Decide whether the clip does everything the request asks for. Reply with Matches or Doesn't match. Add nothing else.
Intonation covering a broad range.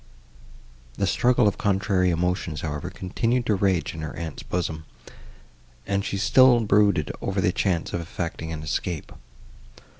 Doesn't match